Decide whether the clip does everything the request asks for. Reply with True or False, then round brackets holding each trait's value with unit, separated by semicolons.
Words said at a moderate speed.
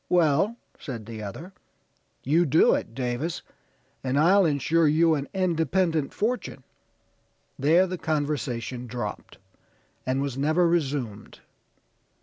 False (115 wpm)